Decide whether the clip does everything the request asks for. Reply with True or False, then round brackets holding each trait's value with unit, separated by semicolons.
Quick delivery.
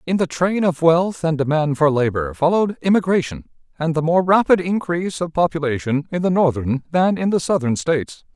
False (185 wpm)